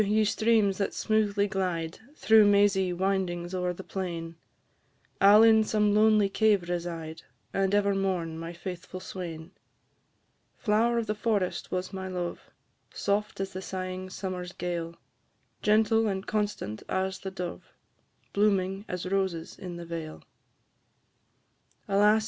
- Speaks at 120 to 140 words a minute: Yes, slow, 135 wpm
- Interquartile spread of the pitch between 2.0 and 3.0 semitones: Yes, average, 2.7 semitones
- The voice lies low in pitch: No, high, 190 Hz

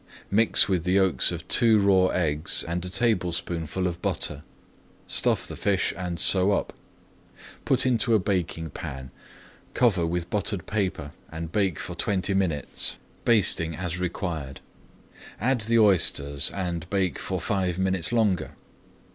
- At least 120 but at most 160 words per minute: Yes, average, 140 wpm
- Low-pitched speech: Yes, very low, 90 Hz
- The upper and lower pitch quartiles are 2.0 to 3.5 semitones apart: Yes, average, 3.1 semitones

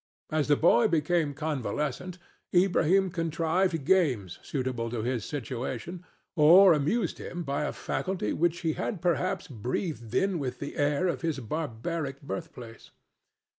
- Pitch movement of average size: Yes, average, 5.0 semitones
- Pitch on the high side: No, medium, 155 Hz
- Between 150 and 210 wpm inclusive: No, slow, 135 wpm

